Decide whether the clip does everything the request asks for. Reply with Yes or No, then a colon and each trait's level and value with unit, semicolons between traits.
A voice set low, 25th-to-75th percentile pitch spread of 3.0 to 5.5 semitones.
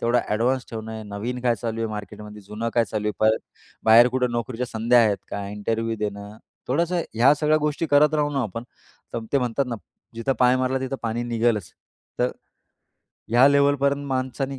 Yes: low, 120 Hz; average, 3.3 semitones